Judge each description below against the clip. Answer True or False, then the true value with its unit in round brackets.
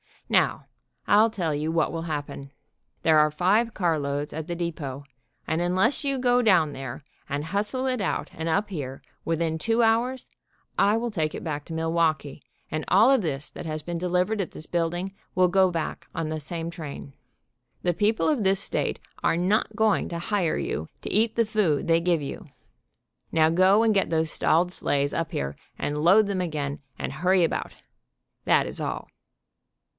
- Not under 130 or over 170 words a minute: False (185 wpm)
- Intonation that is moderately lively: True (4.6 semitones)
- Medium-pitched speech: True (170 Hz)